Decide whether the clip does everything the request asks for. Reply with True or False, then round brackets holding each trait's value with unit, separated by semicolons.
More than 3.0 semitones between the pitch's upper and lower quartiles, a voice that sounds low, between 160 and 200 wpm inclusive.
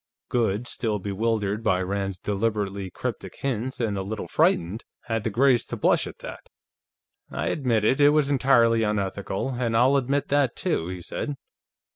True (4.4 semitones; 115 Hz; 165 wpm)